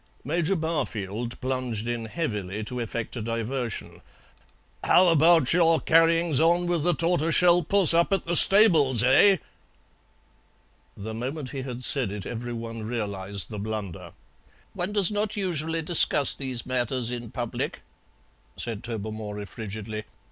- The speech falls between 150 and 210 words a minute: No, slow, 135 wpm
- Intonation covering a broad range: Yes, wide, 6.8 semitones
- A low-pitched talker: Yes, low, 130 Hz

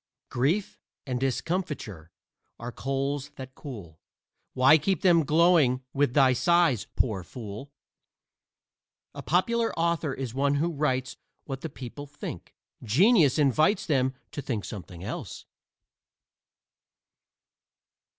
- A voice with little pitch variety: No, average, 4.5 semitones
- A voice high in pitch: No, low, 135 Hz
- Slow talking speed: Yes, slow, 110 wpm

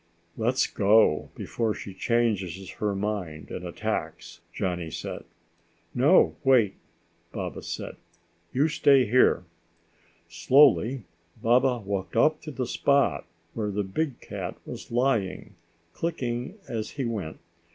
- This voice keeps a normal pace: No, slow, 120 wpm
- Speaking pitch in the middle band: No, low, 115 Hz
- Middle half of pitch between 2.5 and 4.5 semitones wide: No, average, 5.2 semitones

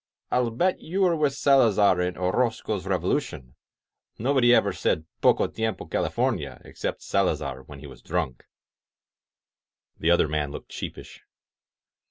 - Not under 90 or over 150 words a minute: Yes, average, 140 wpm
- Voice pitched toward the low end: Yes, low, 105 Hz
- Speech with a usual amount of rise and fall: No, wide, 8.4 semitones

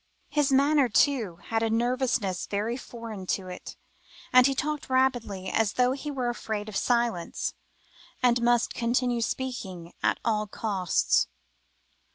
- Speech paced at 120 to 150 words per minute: Yes, average, 140 wpm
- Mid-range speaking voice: No, high, 235 Hz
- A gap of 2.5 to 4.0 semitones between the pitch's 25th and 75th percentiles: Yes, average, 3.6 semitones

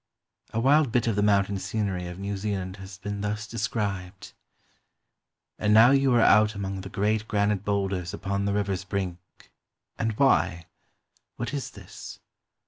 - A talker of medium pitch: No, low, 100 Hz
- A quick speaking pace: No, average, 165 wpm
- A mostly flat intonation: Yes, narrow, 2.0 semitones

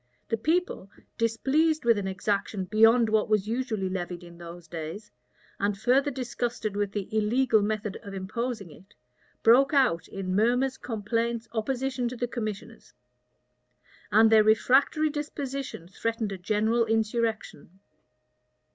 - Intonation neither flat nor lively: Yes, average, 3.6 semitones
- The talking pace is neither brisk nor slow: No, slow, 130 wpm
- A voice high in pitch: Yes, high, 220 Hz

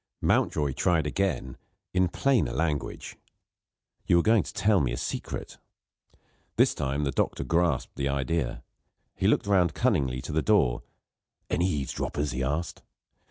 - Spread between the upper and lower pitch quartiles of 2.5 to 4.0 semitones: No, average, 4.8 semitones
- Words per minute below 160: Yes, average, 145 wpm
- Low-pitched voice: Yes, very low, 75 Hz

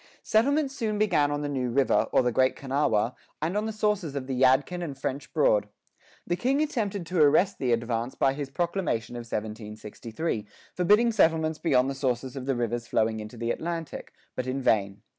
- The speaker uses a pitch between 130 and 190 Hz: Yes, medium, 140 Hz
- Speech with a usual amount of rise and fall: No, wide, 6.5 semitones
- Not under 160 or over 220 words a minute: Yes, average, 190 wpm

